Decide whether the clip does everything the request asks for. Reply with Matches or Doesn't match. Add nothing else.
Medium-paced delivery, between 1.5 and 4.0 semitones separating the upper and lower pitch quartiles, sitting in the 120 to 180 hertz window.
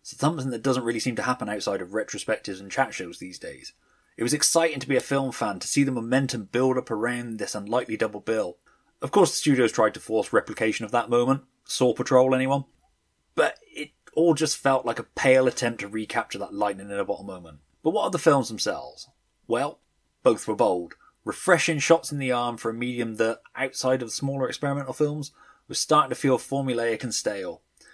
Doesn't match